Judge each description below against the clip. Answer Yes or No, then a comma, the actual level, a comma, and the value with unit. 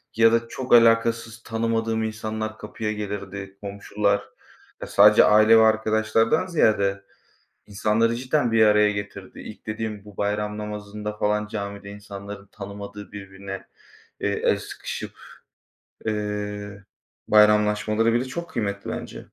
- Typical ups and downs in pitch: No, narrow, 1.8 semitones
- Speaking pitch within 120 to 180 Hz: No, low, 105 Hz